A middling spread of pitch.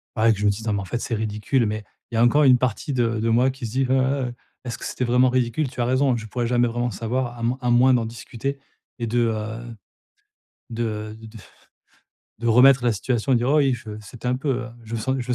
No: narrow, 2.3 semitones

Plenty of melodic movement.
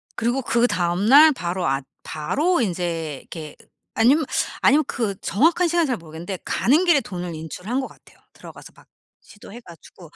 Yes: wide, 8.0 semitones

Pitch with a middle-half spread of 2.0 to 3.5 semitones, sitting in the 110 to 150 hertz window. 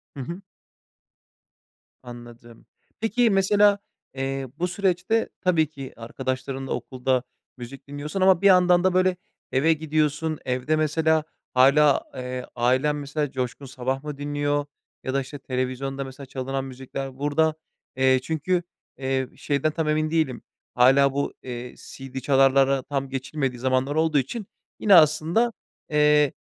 Yes: average, 3.2 semitones; medium, 140 Hz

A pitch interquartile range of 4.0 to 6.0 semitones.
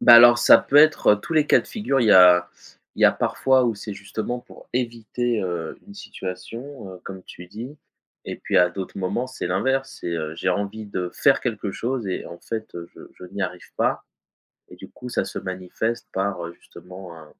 Yes: average, 5.0 semitones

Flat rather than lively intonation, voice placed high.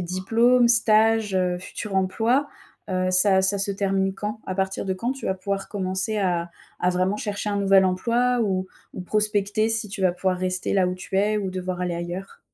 Yes: narrow, 2.3 semitones; high, 195 Hz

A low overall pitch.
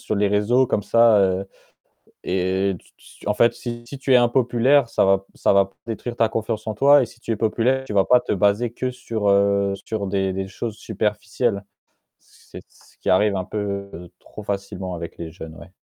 Yes: low, 105 Hz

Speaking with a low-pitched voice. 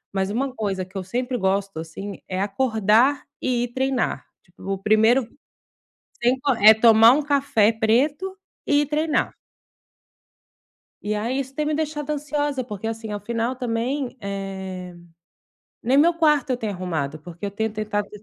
No: high, 230 Hz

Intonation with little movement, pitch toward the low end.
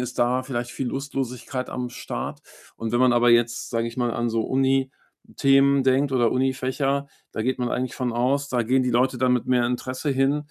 Yes: narrow, 1.8 semitones; low, 130 Hz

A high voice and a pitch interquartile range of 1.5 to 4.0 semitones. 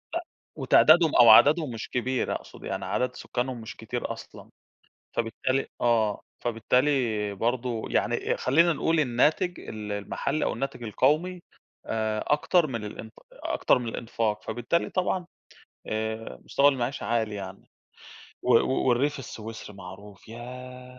No: low, 120 Hz; average, 3.7 semitones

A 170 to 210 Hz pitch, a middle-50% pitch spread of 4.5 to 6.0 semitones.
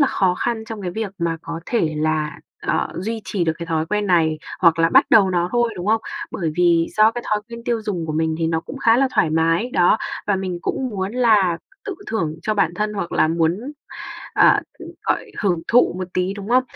Yes: medium, 185 Hz; average, 4.9 semitones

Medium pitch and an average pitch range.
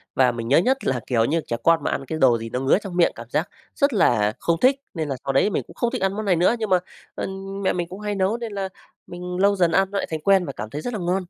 No: medium, 175 Hz; wide, 6.6 semitones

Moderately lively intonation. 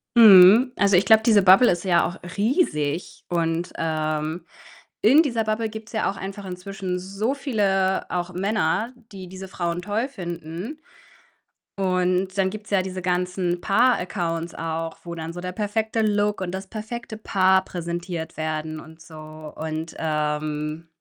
Yes: average, 3.7 semitones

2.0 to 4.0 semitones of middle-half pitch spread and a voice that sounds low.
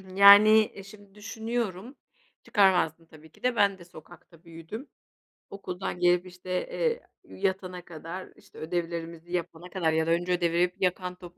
No: average, 2.8 semitones; medium, 180 Hz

